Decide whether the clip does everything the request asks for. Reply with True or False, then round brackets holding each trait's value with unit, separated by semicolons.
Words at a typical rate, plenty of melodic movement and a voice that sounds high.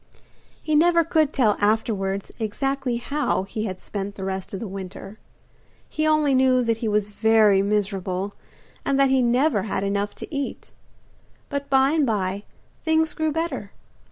True (160 wpm; 5.8 semitones; 225 Hz)